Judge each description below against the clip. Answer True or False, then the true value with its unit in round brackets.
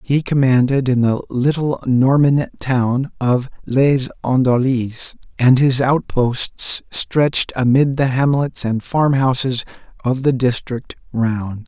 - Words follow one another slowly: True (120 wpm)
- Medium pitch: False (130 Hz)